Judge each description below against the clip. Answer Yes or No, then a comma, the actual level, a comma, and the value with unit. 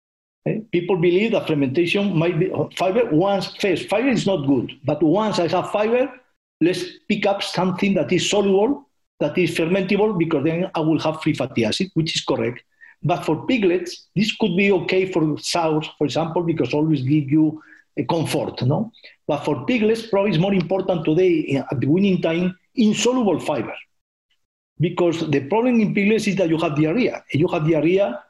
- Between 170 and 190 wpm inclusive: Yes, average, 180 wpm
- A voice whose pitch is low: No, medium, 180 Hz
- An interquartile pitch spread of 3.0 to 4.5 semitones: Yes, average, 4.1 semitones